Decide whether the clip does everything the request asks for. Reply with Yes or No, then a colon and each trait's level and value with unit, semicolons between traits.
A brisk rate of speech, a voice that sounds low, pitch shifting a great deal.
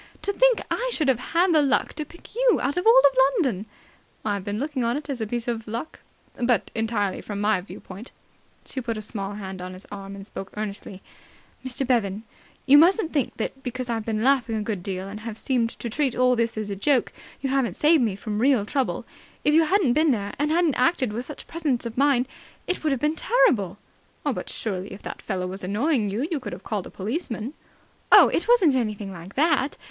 No: fast, 220 wpm; high, 240 Hz; wide, 5.9 semitones